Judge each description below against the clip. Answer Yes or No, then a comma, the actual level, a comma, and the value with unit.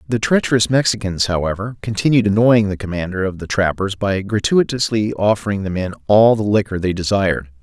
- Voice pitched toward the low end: Yes, low, 100 Hz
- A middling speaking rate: Yes, average, 165 wpm